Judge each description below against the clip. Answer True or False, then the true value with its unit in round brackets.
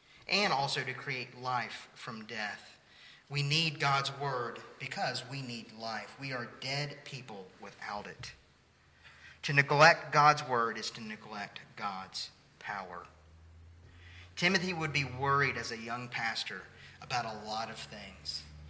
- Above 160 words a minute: False (140 wpm)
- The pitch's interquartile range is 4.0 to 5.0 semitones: True (4.4 semitones)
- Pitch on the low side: True (125 Hz)